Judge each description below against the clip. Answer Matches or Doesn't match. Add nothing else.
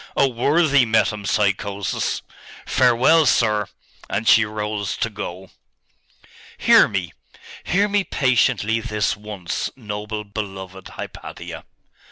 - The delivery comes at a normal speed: Doesn't match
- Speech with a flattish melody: Doesn't match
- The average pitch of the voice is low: Matches